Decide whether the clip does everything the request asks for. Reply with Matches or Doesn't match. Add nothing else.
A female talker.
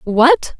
Matches